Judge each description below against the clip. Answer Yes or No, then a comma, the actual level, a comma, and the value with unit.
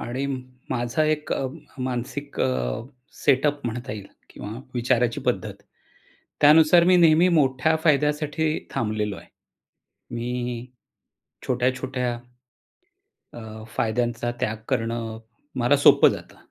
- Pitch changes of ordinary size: Yes, average, 3.8 semitones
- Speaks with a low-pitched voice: Yes, low, 125 Hz